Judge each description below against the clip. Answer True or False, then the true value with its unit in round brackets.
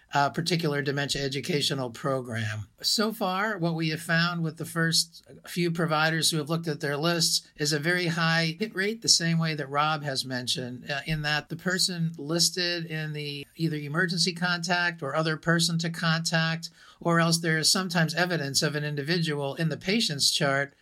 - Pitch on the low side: False (160 Hz)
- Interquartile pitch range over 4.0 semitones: False (2.6 semitones)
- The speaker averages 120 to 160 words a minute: False (185 wpm)